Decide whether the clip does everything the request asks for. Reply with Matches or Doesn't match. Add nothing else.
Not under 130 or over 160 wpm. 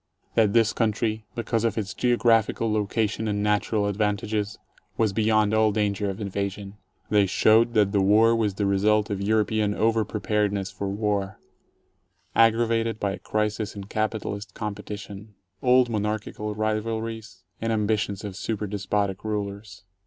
Matches